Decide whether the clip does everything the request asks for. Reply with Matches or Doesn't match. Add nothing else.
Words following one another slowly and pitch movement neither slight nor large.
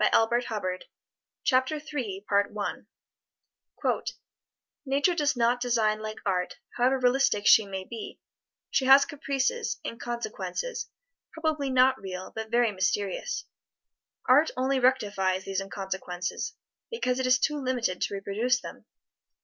Matches